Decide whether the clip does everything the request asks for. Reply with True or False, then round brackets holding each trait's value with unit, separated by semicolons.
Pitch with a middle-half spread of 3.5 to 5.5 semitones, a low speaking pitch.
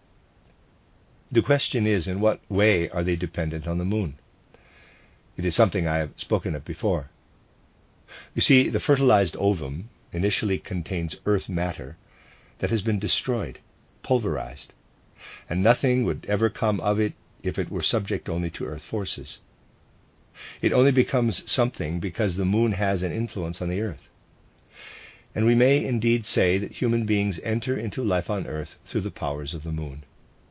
True (4.6 semitones; 100 Hz)